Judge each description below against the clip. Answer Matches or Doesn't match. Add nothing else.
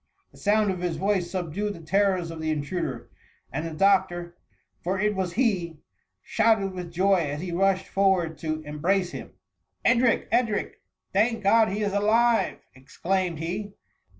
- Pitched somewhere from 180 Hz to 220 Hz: Matches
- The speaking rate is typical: Matches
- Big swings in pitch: Doesn't match